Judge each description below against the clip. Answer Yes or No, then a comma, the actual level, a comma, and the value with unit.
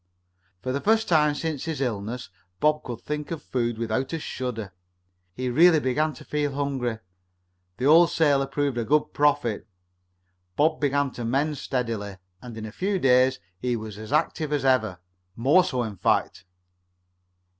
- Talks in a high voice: No, low, 135 Hz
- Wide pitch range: No, average, 4.2 semitones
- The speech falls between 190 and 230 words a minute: No, average, 165 wpm